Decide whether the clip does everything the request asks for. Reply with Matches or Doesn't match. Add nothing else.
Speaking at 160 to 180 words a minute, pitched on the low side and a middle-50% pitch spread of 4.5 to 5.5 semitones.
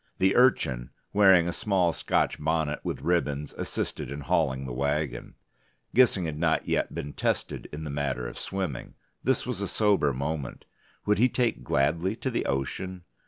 Matches